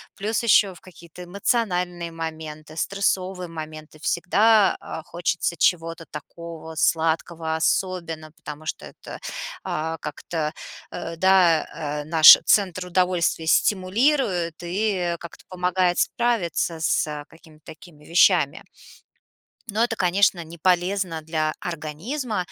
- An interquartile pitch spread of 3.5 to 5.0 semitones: No, average, 2.7 semitones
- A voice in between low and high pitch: Yes, medium, 175 Hz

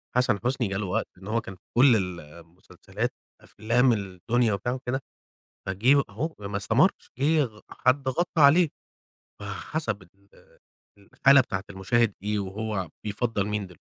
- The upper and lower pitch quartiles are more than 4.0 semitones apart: Yes, average, 4.5 semitones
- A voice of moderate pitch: No, low, 105 Hz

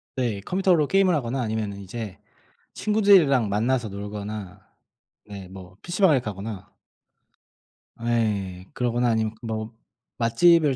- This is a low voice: Yes, low, 115 Hz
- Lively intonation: No, average, 5.0 semitones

